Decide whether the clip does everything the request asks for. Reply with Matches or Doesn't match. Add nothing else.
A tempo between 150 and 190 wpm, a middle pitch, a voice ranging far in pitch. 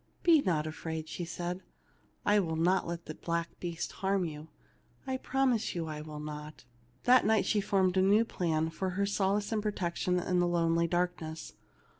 Doesn't match